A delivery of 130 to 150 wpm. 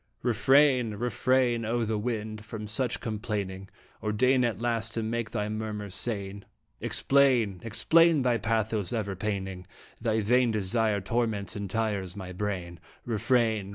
Yes: slow, 135 wpm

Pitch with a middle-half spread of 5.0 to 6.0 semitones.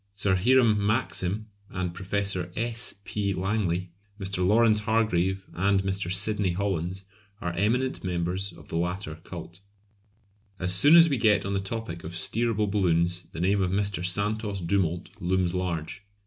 No: average, 2.8 semitones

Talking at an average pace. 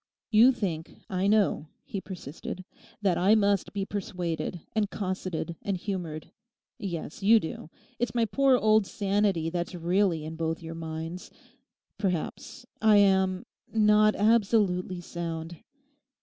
No: slow, 125 wpm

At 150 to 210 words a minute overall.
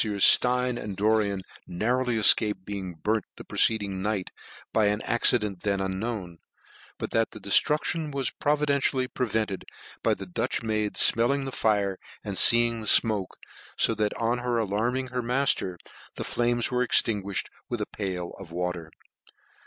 Yes: average, 160 wpm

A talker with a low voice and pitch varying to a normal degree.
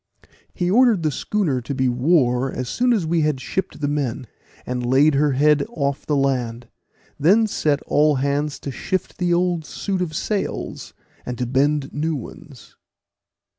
No: medium, 150 Hz; average, 4.6 semitones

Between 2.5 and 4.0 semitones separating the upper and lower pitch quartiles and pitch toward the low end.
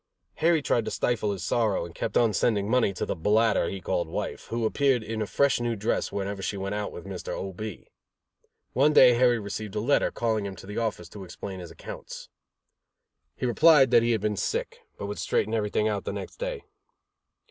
Yes: average, 3.1 semitones; low, 110 Hz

